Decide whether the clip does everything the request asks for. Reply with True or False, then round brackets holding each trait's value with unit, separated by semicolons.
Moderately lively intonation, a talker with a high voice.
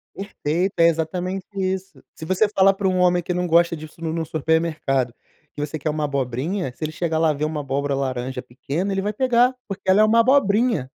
False (4.3 semitones; 170 Hz)